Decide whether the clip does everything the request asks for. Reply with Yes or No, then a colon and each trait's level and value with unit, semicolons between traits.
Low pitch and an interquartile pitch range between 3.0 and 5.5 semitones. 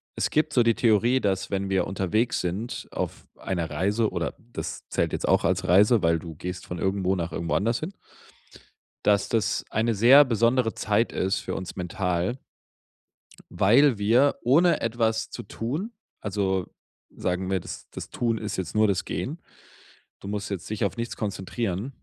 Yes: low, 105 Hz; average, 3.9 semitones